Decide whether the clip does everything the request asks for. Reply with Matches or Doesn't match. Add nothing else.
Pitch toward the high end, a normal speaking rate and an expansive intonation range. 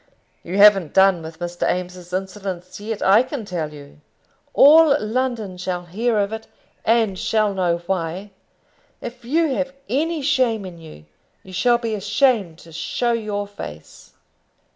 Doesn't match